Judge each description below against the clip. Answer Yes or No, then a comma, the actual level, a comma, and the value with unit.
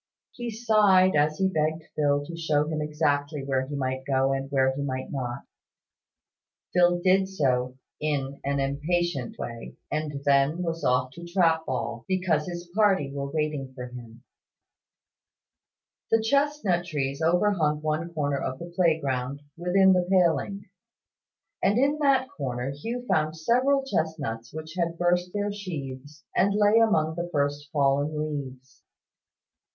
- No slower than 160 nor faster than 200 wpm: No, average, 145 wpm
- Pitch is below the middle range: No, medium, 155 Hz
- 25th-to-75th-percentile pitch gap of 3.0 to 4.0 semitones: No, average, 4.6 semitones